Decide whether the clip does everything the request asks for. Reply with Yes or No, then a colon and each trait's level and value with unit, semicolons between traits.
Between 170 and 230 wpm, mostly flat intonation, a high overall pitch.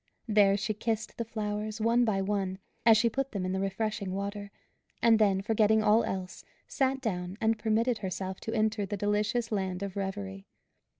Yes: average, 180 wpm; narrow, 2.3 semitones; high, 210 Hz